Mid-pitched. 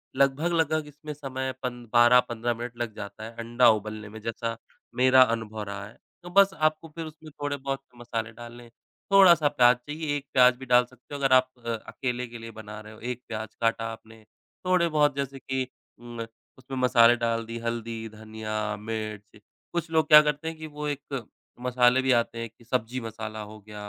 No: low, 125 Hz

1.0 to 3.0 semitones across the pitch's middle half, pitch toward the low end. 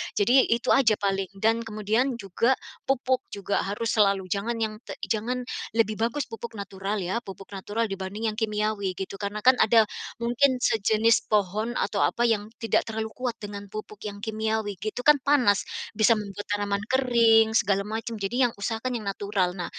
No: narrow, 2.4 semitones; high, 215 Hz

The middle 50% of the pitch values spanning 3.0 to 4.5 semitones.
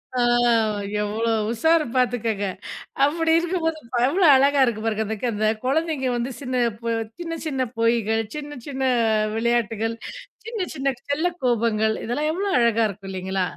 No: average, 5.3 semitones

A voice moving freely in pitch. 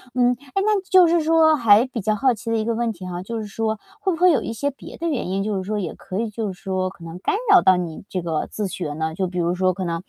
Yes: wide, 5.8 semitones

